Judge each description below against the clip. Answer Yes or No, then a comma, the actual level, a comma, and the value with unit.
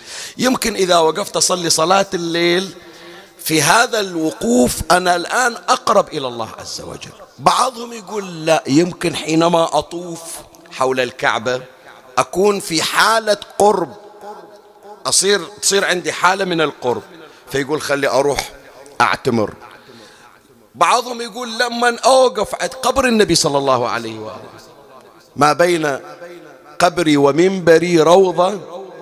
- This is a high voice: No, medium, 175 Hz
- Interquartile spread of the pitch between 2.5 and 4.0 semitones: No, average, 4.7 semitones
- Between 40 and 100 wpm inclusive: No, average, 110 wpm